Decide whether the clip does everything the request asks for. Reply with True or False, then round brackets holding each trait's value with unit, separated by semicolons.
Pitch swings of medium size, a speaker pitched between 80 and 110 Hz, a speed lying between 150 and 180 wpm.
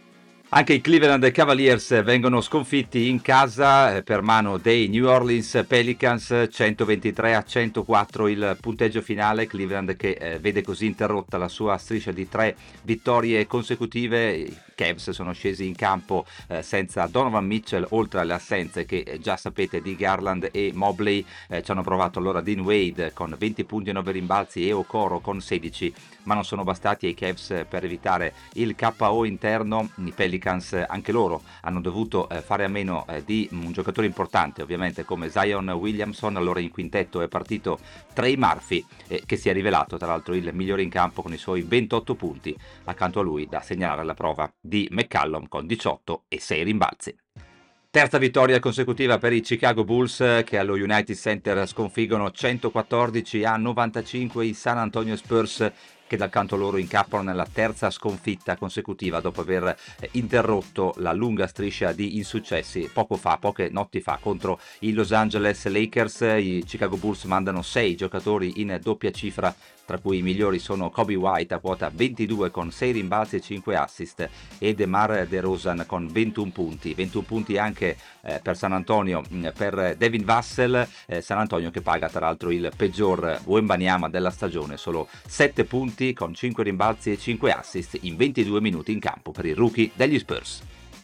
True (3.5 semitones; 105 Hz; 160 wpm)